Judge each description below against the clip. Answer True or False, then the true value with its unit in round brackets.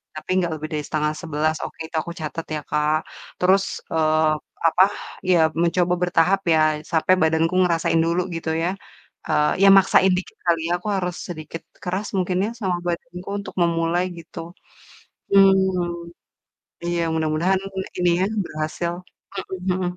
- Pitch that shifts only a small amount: True (2.3 semitones)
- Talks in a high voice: False (170 Hz)